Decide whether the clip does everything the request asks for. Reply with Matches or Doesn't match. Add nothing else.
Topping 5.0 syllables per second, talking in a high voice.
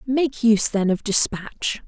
Doesn't match